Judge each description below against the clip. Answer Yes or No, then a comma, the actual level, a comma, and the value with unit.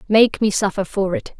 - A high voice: Yes, high, 205 Hz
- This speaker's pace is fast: Yes, fast, 215 wpm